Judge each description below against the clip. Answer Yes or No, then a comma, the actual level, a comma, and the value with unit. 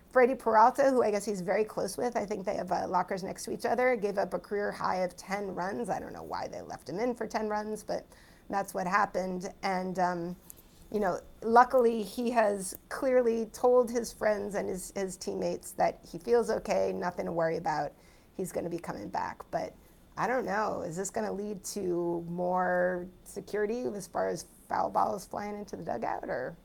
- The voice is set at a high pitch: Yes, high, 205 Hz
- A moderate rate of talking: No, fast, 210 wpm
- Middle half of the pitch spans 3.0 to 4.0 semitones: Yes, average, 3.6 semitones